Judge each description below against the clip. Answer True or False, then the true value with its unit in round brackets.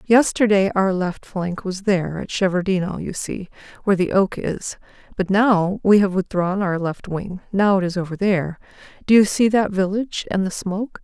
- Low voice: False (195 Hz)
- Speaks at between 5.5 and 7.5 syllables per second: False (5.0 syllables/s)